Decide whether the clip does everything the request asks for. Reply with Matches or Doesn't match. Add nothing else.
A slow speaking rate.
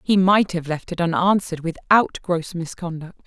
Doesn't match